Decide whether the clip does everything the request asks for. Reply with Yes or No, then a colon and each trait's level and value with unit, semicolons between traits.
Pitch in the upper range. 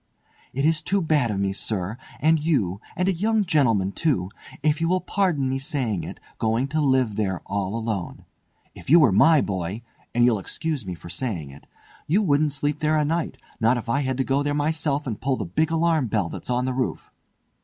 No: low, 135 Hz